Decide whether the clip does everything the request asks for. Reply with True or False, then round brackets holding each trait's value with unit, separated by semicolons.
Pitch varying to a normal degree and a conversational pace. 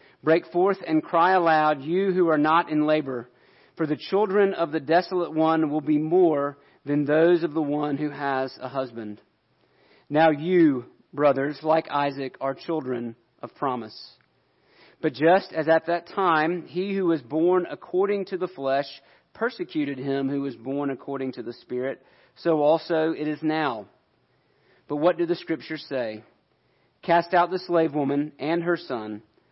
True (3.6 semitones; 165 wpm)